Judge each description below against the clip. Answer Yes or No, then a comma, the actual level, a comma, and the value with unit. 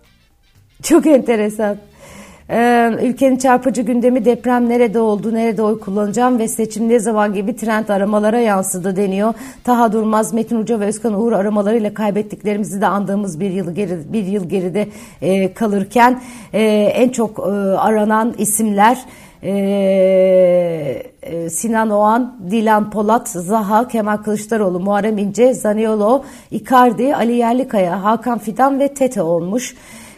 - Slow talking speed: No, average, 120 wpm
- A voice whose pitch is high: Yes, high, 215 Hz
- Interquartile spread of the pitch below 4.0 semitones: Yes, average, 2.9 semitones